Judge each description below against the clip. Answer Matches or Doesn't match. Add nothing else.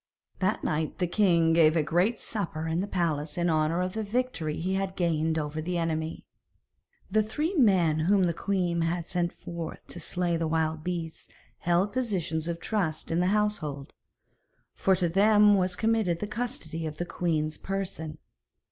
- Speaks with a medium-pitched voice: Matches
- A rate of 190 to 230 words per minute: Doesn't match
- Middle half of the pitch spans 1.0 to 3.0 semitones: Doesn't match